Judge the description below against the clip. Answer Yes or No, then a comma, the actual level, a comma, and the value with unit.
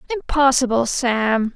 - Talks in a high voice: Yes, very high, 255 Hz